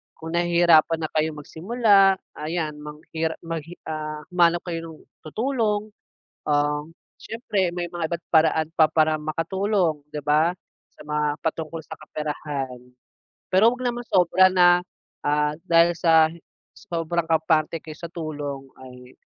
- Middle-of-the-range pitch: Yes, medium, 165 Hz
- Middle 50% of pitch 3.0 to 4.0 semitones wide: No, narrow, 2.5 semitones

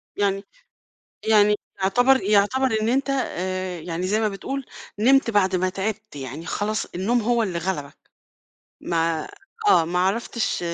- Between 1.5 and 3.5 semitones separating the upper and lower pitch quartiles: No, average, 4.0 semitones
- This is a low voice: No, high, 200 Hz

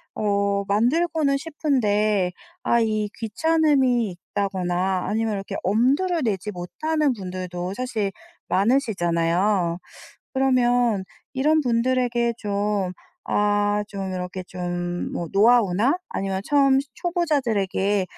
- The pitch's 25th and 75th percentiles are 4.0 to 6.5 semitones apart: Yes, wide, 5.4 semitones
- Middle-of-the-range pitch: No, high, 210 Hz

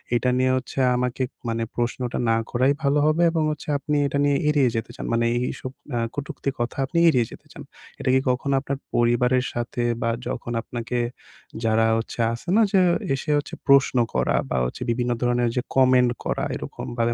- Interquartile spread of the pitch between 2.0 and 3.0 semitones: Yes, narrow, 2.5 semitones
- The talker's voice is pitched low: Yes, low, 125 Hz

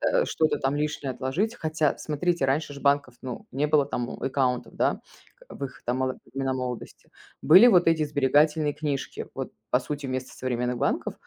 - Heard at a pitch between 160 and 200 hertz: No, medium, 140 Hz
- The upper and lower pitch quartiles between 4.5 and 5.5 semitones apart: No, average, 2.8 semitones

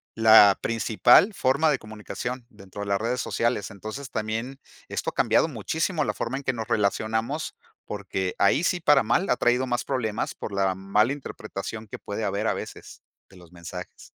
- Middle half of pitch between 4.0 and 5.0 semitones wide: Yes, average, 4.3 semitones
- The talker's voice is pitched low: Yes, low, 110 Hz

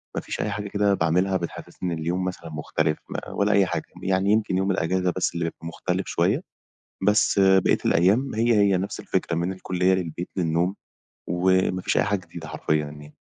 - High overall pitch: No, very low, 95 Hz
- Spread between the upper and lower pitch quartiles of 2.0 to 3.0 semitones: Yes, narrow, 2.6 semitones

